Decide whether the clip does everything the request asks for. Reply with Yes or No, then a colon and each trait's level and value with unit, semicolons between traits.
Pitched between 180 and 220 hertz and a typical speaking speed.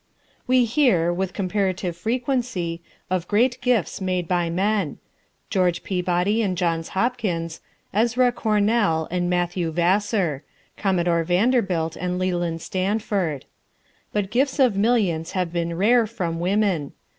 No: medium, 185 Hz; slow, 125 wpm